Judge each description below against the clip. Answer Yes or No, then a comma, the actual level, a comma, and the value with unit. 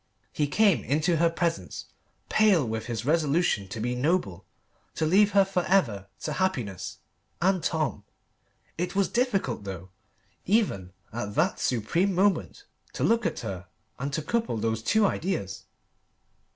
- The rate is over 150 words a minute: No, average, 145 wpm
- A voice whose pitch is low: No, medium, 155 Hz